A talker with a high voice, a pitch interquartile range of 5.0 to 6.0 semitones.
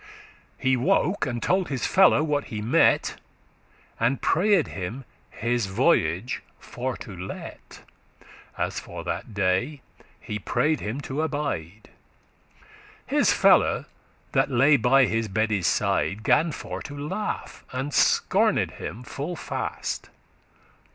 No: low, 130 Hz; wide, 5.4 semitones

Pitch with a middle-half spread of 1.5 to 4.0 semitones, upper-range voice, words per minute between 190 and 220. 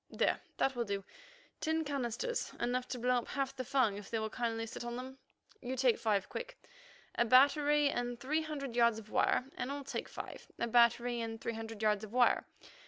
Yes: average, 3.1 semitones; high, 245 Hz; fast, 205 wpm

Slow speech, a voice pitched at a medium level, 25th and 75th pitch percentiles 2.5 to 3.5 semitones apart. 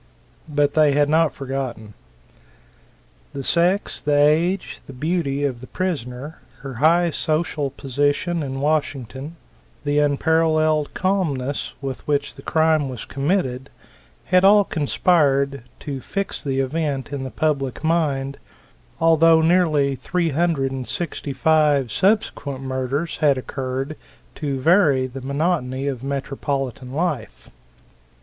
Yes: slow, 125 wpm; medium, 145 Hz; average, 3.2 semitones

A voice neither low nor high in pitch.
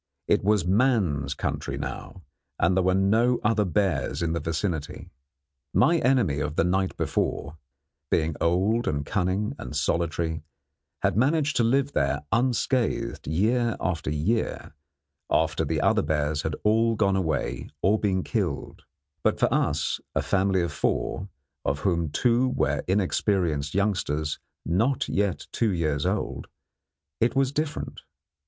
No: very low, 95 Hz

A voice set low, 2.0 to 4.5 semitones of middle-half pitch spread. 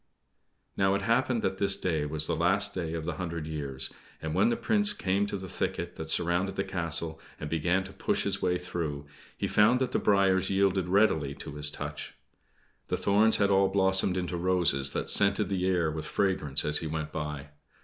Yes: very low, 90 Hz; average, 3.8 semitones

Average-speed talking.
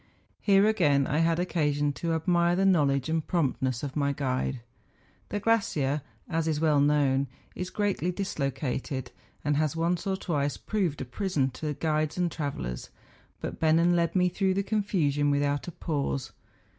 Yes: average, 160 wpm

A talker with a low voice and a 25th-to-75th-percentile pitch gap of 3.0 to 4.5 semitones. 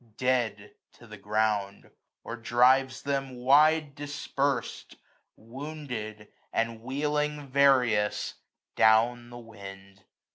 Yes: low, 120 Hz; average, 4.1 semitones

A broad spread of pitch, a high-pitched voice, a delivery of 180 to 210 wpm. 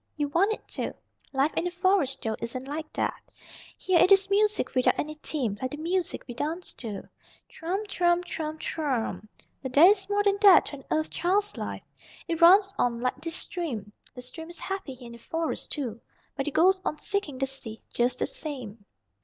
Yes: wide, 6.5 semitones; very high, 310 Hz; fast, 205 wpm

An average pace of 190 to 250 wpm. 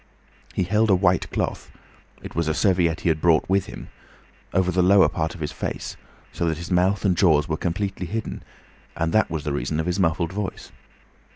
Yes: average, 195 wpm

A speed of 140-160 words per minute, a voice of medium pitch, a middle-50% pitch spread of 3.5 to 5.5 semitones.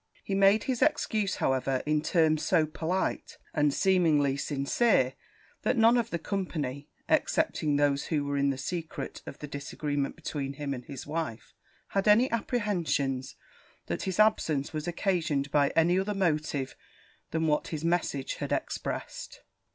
Yes: average, 150 wpm; medium, 155 Hz; average, 5.1 semitones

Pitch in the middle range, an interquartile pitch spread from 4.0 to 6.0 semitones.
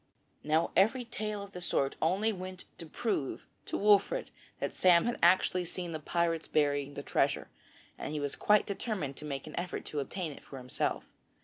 Yes: medium, 175 Hz; average, 4.9 semitones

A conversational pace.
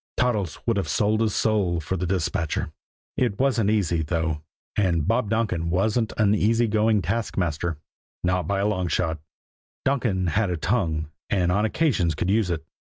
Yes: average, 165 wpm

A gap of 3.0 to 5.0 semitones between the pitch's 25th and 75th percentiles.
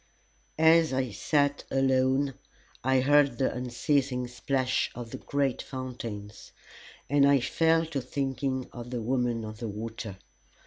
No: narrow, 2.6 semitones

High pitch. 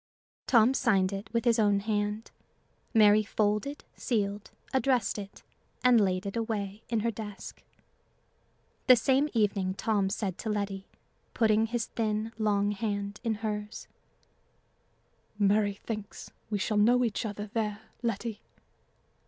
Yes: high, 210 Hz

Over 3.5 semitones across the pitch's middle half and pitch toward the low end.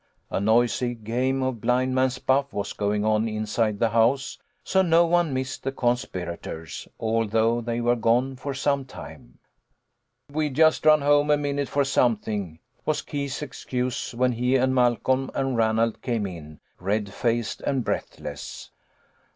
No: average, 3.2 semitones; low, 125 Hz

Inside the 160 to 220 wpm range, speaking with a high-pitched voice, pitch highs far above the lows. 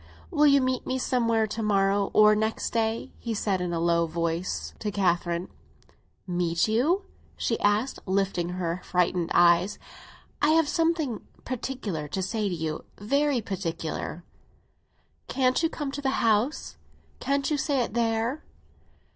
No: average, 145 wpm; high, 215 Hz; wide, 6.4 semitones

